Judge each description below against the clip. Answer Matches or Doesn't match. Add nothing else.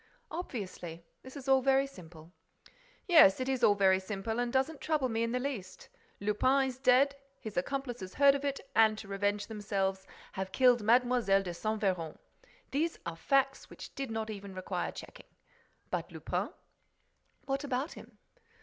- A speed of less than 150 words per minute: Doesn't match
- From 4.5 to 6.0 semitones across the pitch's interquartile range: Matches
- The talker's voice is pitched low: Doesn't match